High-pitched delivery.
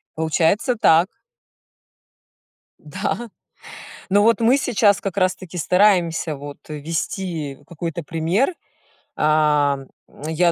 No: medium, 170 Hz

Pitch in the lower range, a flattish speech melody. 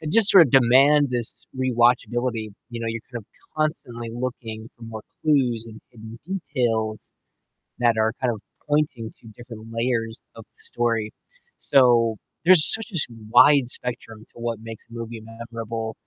Yes: low, 120 Hz; narrow, 2.3 semitones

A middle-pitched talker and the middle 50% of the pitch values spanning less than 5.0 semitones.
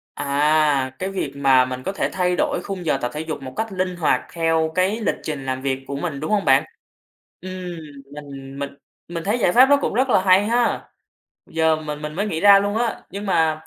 No: medium, 160 Hz; wide, 5.6 semitones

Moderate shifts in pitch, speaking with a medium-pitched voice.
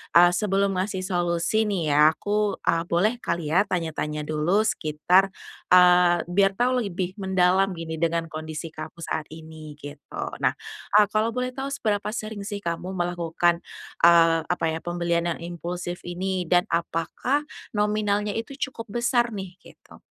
Yes: average, 3.4 semitones; medium, 180 Hz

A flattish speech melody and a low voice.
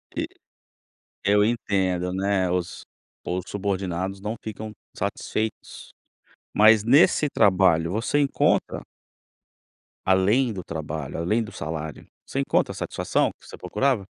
No: average, 3.4 semitones; very low, 95 Hz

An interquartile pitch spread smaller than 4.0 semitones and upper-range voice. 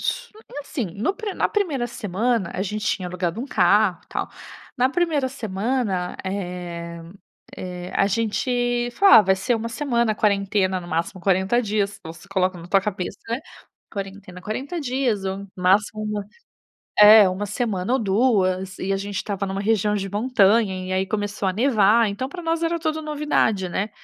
No: average, 4.3 semitones; high, 205 Hz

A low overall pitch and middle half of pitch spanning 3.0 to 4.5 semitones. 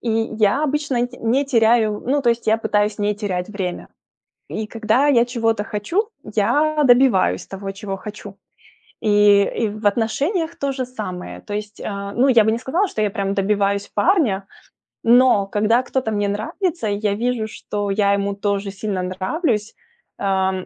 No: high, 215 Hz; average, 3.5 semitones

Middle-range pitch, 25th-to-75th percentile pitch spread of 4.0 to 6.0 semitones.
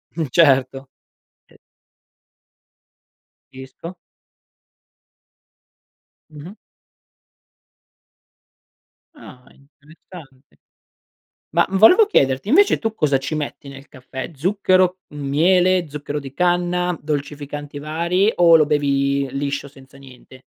Yes: medium, 150 Hz; average, 4.3 semitones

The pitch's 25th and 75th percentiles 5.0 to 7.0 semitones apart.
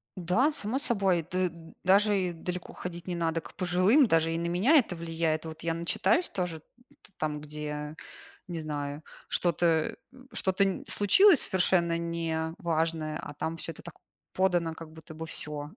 No: average, 2.7 semitones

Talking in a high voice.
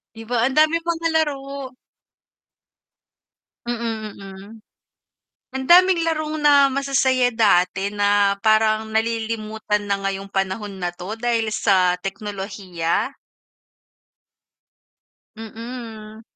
Yes: high, 220 Hz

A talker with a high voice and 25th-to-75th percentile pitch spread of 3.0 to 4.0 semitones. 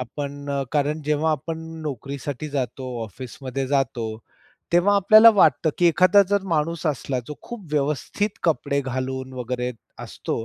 No: medium, 145 Hz; average, 3.5 semitones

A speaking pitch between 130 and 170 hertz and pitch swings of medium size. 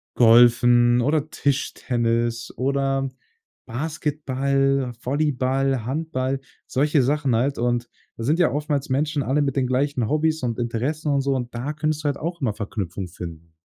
Yes: low, 135 Hz; average, 3.2 semitones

